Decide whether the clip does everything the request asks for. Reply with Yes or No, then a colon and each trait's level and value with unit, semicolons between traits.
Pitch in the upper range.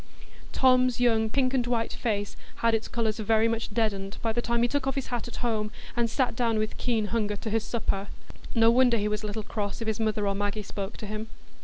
Yes: high, 225 Hz